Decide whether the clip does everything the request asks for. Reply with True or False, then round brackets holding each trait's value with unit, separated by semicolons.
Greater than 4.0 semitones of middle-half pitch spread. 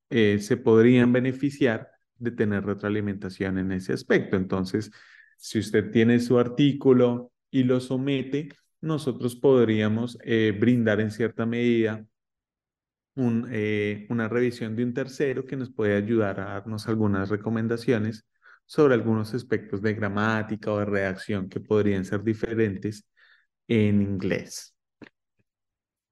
False (2.8 semitones)